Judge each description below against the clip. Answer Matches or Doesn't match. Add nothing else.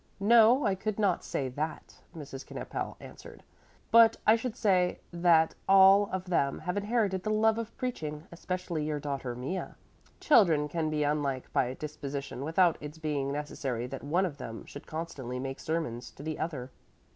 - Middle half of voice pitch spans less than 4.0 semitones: Doesn't match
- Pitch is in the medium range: Matches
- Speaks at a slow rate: Doesn't match